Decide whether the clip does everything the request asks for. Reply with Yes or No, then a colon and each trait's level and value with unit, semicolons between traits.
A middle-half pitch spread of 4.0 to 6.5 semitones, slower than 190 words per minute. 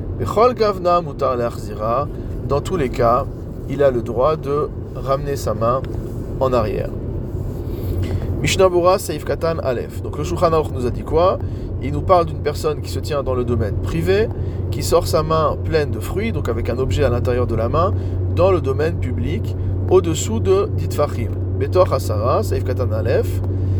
Yes: average, 4.3 semitones; average, 165 wpm